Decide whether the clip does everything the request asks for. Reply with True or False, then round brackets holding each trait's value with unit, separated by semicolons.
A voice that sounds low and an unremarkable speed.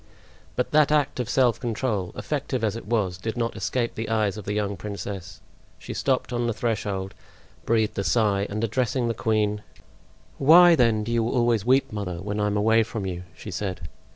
True (110 Hz; 195 wpm)